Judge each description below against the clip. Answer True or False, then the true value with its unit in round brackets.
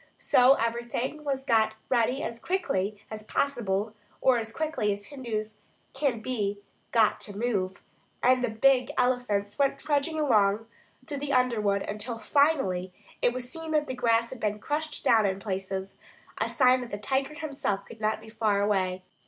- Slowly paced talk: False (170 wpm)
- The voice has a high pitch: True (230 Hz)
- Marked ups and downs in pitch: False (4.5 semitones)